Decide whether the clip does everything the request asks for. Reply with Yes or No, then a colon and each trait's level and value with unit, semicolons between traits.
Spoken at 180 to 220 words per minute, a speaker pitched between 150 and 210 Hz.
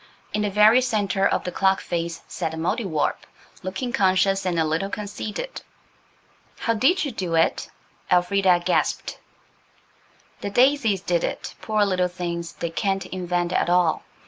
No: average, 150 wpm; high, 190 Hz